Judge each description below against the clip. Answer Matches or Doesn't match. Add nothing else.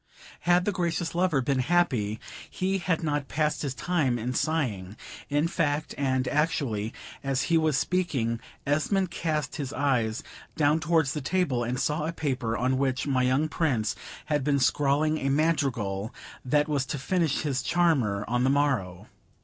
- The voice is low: Doesn't match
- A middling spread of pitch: Matches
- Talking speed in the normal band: Matches